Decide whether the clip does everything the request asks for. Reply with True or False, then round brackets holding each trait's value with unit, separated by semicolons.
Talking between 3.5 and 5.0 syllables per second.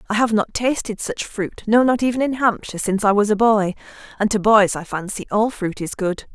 False (5.5 syllables/s)